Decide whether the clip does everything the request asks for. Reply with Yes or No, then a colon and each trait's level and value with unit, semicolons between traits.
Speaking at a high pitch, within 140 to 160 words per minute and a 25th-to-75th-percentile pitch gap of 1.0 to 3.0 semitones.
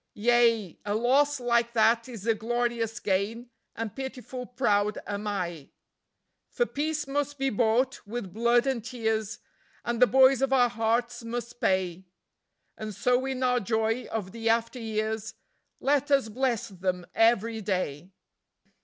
Yes: high, 230 Hz; average, 145 wpm; average, 2.7 semitones